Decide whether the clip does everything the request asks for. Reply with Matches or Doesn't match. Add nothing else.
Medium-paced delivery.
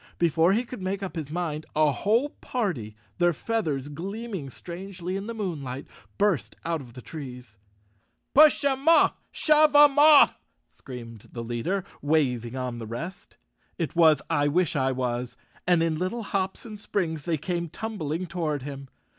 Matches